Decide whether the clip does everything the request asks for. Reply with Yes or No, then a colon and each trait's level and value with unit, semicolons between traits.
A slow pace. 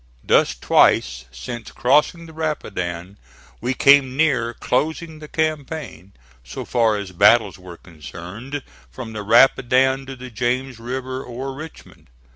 Yes: slow, 130 wpm